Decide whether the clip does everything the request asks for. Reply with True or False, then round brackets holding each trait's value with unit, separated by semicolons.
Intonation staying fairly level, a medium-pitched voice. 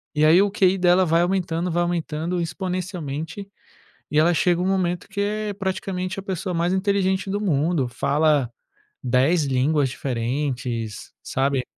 False (4.5 semitones; 175 Hz)